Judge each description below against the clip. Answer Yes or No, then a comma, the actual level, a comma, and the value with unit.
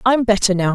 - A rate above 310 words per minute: Yes, fast, 320 wpm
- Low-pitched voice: No, high, 210 Hz